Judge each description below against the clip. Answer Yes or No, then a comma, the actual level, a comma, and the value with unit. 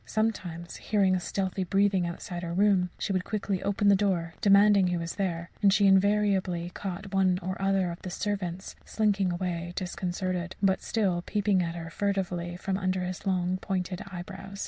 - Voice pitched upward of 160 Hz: Yes, high, 190 Hz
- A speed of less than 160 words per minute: No, average, 175 wpm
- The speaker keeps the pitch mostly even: Yes, narrow, 2.0 semitones